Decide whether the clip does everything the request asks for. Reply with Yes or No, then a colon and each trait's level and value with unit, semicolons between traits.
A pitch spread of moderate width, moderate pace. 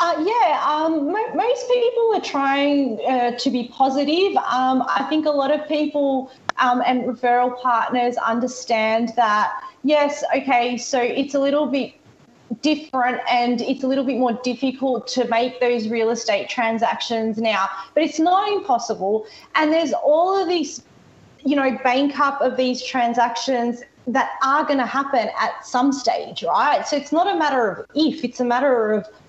Yes: average, 3.6 semitones; average, 170 wpm